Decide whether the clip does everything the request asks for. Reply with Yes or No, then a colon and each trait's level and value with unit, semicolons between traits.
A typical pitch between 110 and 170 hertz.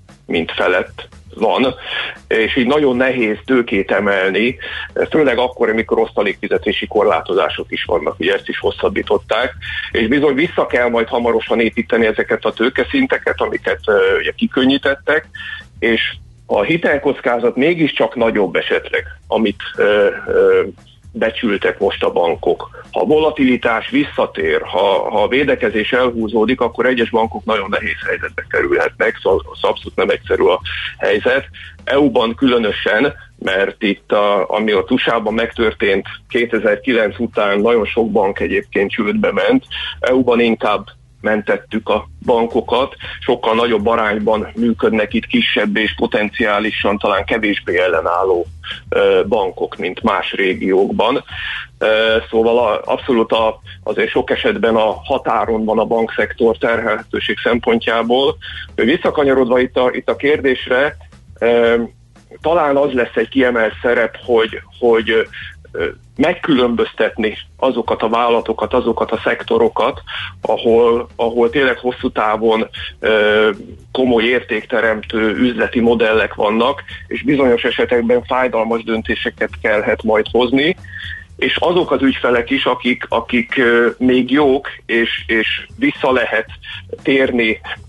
Yes: low, 130 Hz